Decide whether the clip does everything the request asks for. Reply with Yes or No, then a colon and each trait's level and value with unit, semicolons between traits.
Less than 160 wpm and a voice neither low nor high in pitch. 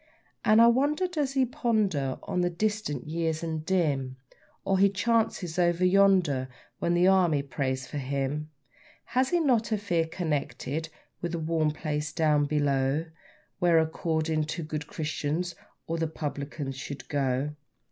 Yes: average, 150 wpm; medium, 160 Hz